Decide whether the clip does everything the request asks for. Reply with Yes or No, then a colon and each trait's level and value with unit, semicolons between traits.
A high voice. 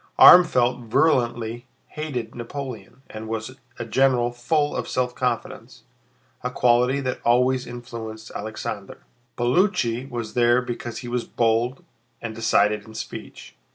No: low, 120 Hz